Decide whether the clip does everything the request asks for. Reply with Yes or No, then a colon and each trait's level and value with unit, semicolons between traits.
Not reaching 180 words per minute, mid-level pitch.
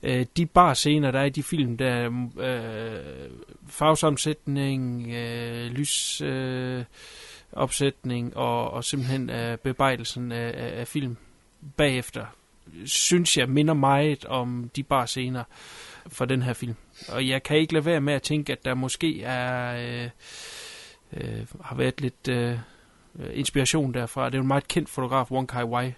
No: average, 150 wpm; low, 130 Hz